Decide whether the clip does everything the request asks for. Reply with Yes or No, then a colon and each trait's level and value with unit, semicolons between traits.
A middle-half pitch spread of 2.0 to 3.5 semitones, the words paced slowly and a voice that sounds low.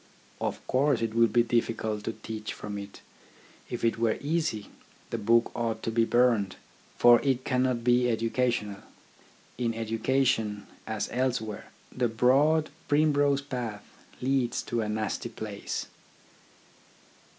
Yes: narrow, 2.6 semitones; slow, 130 wpm; low, 115 Hz